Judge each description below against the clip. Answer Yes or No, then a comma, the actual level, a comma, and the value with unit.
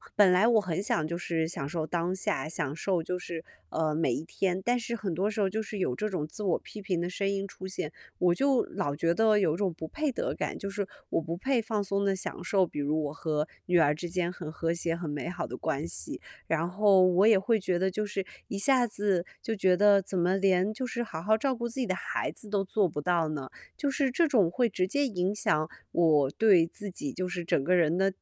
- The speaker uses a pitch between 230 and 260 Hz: No, medium, 185 Hz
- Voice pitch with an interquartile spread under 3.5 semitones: No, average, 4.0 semitones